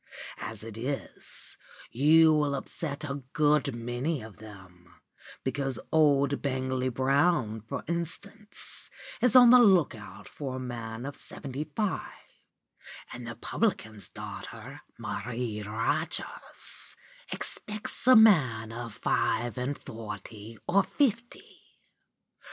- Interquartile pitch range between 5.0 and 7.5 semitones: Yes, wide, 5.6 semitones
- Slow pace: Yes, slow, 115 wpm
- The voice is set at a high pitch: No, low, 130 Hz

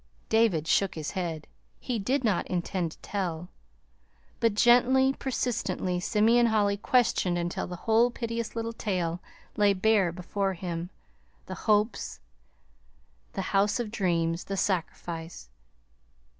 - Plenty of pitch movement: No, average, 4.5 semitones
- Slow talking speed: Yes, slow, 125 wpm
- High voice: Yes, high, 200 Hz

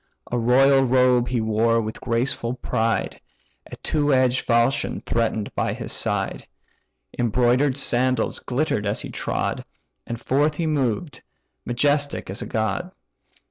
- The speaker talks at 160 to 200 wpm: No, slow, 135 wpm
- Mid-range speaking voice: No, low, 125 Hz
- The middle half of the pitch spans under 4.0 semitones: Yes, average, 2.8 semitones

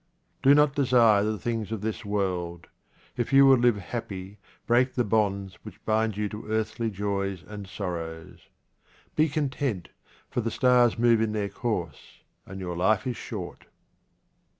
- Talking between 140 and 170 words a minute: Yes, average, 155 wpm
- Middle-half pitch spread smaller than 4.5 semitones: Yes, average, 3.6 semitones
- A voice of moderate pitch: No, low, 110 Hz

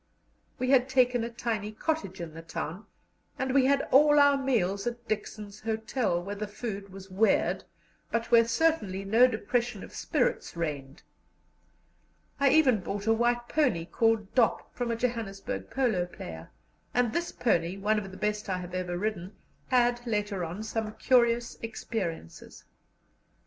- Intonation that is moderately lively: Yes, average, 4.0 semitones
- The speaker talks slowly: No, average, 155 wpm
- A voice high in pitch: Yes, high, 220 Hz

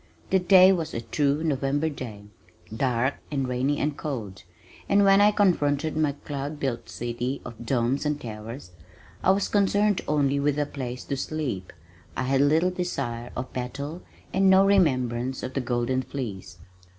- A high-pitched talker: No, medium, 140 Hz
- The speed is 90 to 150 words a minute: No, average, 160 wpm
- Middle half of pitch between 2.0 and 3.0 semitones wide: No, average, 4.1 semitones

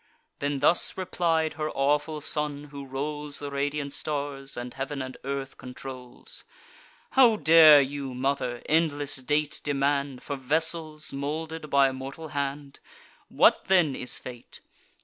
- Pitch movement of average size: No, narrow, 2.0 semitones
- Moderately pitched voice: Yes, medium, 145 Hz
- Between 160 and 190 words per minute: No, slow, 135 wpm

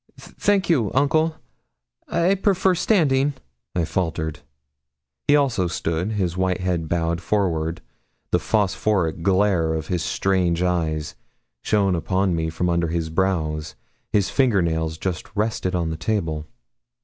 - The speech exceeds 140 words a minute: No, slow, 135 wpm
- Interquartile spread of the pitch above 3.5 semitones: Yes, average, 4.6 semitones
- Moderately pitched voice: No, very low, 90 Hz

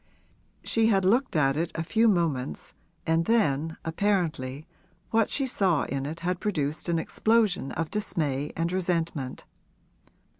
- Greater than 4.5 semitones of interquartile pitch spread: Yes, average, 5.2 semitones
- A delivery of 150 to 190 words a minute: No, average, 140 wpm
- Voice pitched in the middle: Yes, medium, 165 Hz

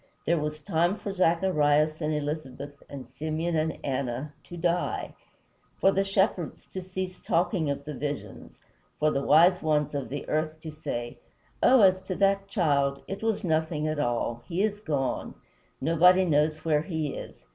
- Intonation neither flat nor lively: Yes, average, 3.7 semitones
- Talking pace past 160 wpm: Yes, average, 170 wpm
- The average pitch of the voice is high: No, medium, 155 Hz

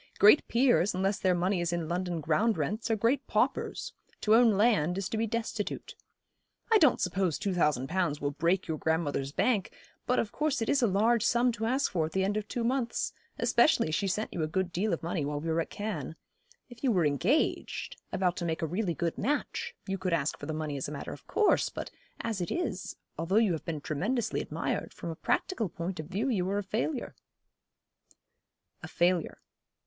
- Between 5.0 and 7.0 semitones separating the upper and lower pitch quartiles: Yes, wide, 5.6 semitones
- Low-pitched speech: No, high, 190 Hz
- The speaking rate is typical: No, fast, 215 wpm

